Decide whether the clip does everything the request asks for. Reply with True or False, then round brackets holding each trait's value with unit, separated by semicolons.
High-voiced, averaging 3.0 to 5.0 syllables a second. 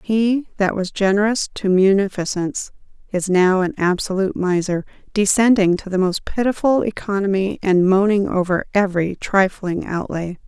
True (195 Hz; 4.9 syllables/s)